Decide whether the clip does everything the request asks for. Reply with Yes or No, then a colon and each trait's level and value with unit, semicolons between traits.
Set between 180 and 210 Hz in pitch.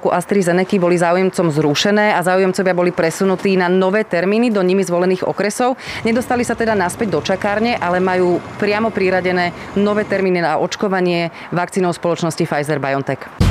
Yes: medium, 185 Hz